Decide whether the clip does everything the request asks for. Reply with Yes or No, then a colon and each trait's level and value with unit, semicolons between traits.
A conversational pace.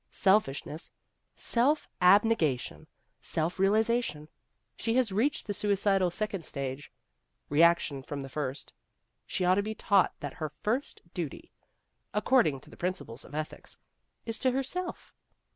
No: slow, 130 wpm